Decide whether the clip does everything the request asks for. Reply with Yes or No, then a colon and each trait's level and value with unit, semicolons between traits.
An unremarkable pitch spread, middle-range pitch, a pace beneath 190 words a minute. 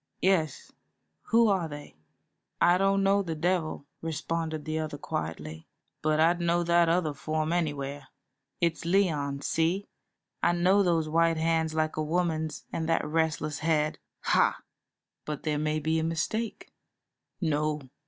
No: narrow, 2.1 semitones; medium, 160 Hz; average, 145 wpm